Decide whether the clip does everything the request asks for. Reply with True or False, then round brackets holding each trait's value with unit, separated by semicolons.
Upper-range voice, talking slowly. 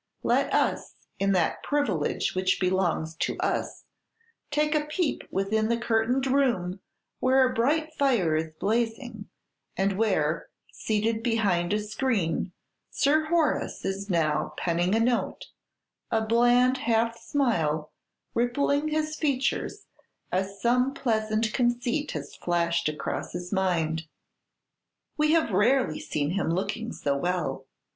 True (220 Hz; 125 wpm)